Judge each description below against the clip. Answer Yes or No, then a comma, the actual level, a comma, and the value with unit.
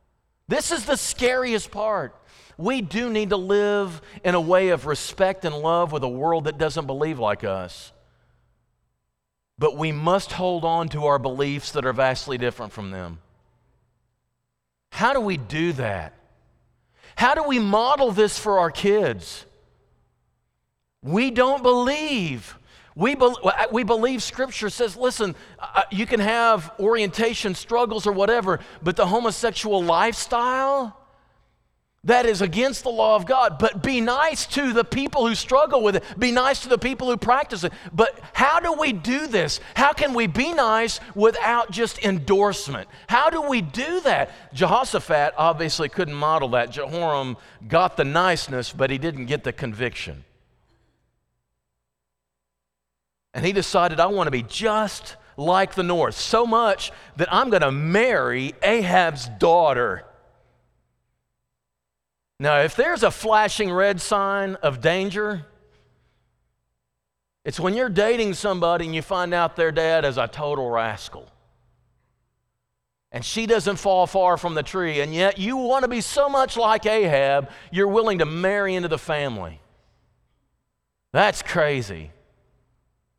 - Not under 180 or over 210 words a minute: No, average, 145 wpm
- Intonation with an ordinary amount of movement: No, wide, 8.5 semitones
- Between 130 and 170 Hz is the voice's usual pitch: No, medium, 185 Hz